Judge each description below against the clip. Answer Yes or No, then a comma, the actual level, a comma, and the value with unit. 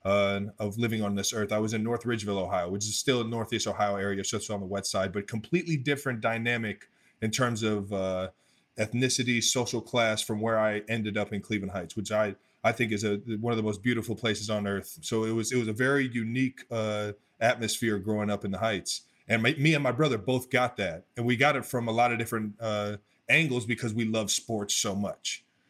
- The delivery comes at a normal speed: No, fast, 230 wpm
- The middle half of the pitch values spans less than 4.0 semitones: Yes, narrow, 2.5 semitones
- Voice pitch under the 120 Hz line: Yes, low, 110 Hz